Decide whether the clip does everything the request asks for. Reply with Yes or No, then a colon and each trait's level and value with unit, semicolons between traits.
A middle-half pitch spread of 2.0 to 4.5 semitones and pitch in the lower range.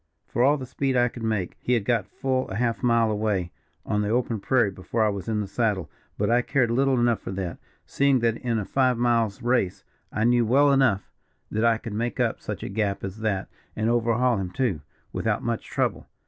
Yes: average, 2.9 semitones; low, 115 Hz